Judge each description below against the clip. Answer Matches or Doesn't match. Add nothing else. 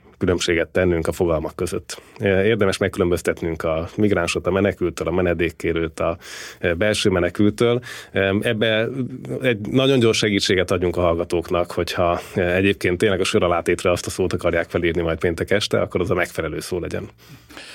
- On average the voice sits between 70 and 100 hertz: Matches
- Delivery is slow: Doesn't match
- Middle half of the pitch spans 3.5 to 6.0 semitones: Matches